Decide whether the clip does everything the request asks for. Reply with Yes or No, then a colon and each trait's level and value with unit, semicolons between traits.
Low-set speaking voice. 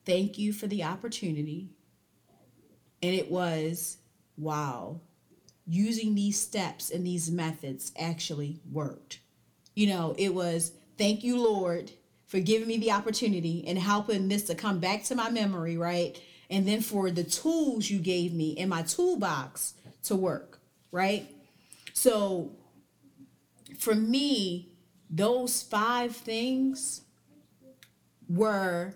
No: high, 190 Hz